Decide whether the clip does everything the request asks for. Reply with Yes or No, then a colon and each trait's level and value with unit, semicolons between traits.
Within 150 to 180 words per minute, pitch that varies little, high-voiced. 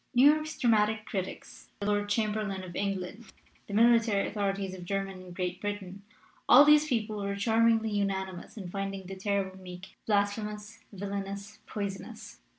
Yes: average, 155 wpm; narrow, 2.1 semitones; high, 200 Hz